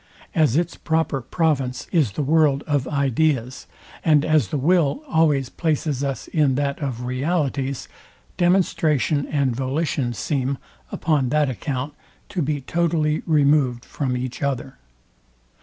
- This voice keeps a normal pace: No, slow, 130 wpm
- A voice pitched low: No, medium, 145 Hz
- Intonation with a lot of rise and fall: No, average, 3.1 semitones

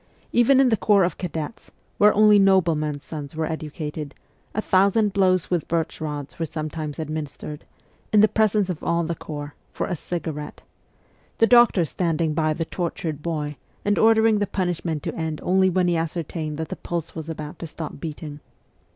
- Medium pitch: Yes, medium, 165 Hz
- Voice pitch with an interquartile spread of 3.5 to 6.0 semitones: Yes, average, 3.8 semitones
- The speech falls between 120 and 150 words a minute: No, average, 175 wpm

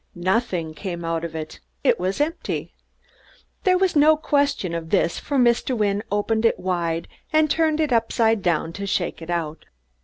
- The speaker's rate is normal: Yes, average, 175 wpm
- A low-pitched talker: No, high, 200 Hz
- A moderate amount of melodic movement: No, wide, 8.9 semitones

